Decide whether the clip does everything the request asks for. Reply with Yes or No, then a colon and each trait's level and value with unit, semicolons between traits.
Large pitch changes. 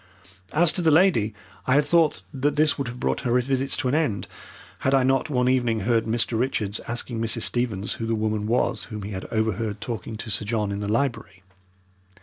No: average, 3.7 semitones